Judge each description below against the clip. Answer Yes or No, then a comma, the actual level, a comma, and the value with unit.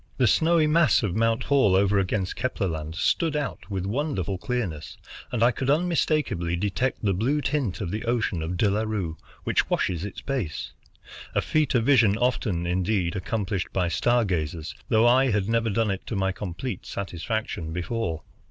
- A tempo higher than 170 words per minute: Yes, average, 180 wpm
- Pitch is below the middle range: Yes, low, 105 Hz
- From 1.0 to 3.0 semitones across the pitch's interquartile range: No, wide, 5.4 semitones